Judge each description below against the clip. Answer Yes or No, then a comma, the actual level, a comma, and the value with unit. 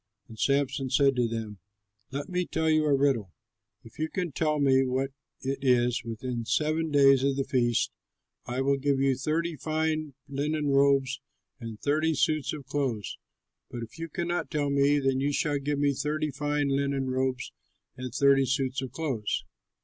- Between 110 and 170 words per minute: No, average, 180 wpm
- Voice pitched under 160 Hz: Yes, medium, 140 Hz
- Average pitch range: No, narrow, 2.3 semitones